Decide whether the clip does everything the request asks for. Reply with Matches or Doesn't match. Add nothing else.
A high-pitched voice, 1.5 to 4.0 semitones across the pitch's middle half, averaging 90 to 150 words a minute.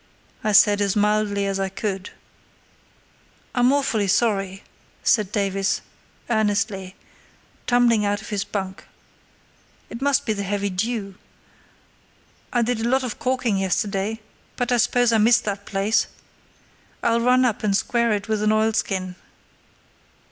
Matches